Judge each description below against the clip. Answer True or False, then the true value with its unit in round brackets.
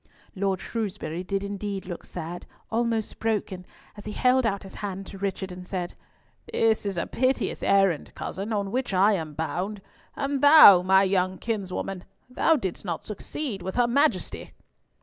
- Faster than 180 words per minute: False (165 wpm)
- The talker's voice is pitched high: True (195 Hz)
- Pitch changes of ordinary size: True (3.3 semitones)